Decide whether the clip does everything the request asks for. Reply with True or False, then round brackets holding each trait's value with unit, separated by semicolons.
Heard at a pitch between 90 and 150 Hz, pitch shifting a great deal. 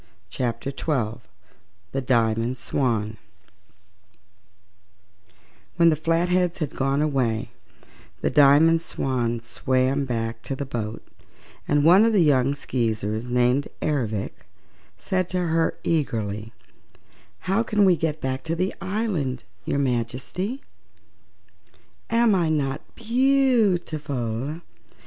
True (140 Hz; 5.9 semitones)